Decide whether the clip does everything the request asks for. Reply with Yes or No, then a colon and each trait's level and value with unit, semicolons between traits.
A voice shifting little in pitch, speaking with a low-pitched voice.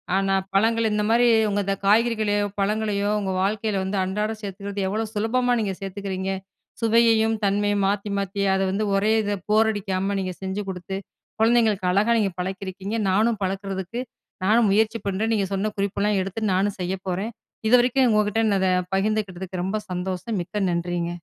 No: narrow, 2.2 semitones; high, 205 Hz